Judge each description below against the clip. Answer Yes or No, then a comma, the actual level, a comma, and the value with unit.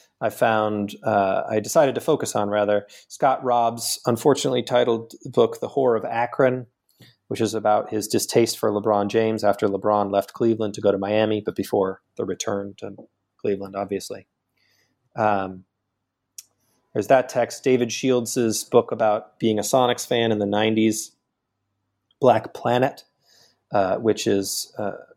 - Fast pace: No, average, 150 wpm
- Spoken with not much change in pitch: No, average, 3.0 semitones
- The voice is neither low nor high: No, low, 110 Hz